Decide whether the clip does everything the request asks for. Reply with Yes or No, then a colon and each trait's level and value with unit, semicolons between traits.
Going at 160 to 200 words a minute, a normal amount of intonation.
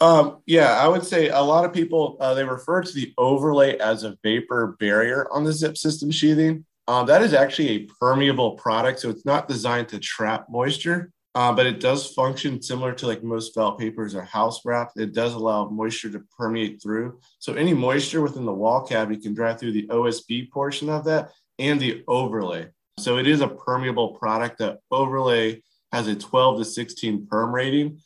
Yes: average, 195 wpm; average, 4.4 semitones